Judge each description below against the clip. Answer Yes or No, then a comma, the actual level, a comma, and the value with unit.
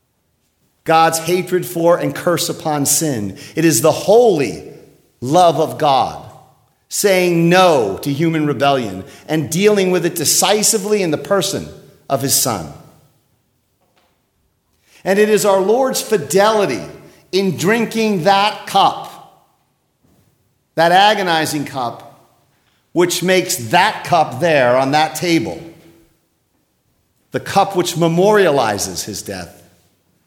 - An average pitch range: No, wide, 5.7 semitones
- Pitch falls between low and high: Yes, medium, 165 Hz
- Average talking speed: No, slow, 115 wpm